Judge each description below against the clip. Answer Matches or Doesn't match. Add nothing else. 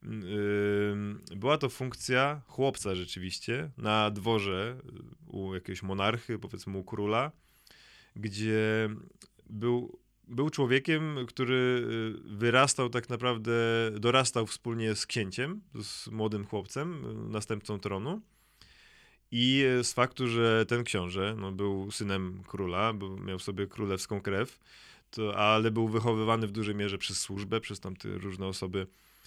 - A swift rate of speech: Doesn't match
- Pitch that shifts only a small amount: Doesn't match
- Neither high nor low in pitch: Doesn't match